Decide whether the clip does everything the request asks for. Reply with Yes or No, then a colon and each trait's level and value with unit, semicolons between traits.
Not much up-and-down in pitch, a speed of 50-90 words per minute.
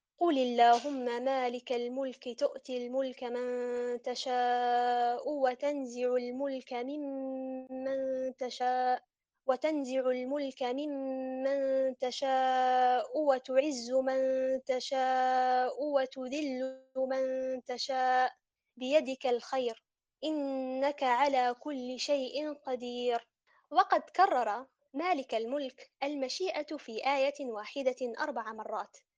Yes: narrow, 1.6 semitones; average, 80 wpm